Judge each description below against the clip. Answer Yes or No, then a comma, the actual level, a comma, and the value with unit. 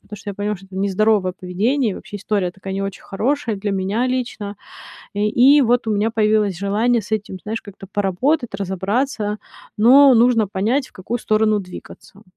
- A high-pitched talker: Yes, high, 210 Hz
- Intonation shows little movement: No, average, 3.1 semitones